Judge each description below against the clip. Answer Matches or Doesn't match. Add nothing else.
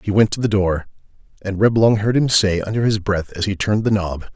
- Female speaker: Doesn't match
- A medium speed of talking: Doesn't match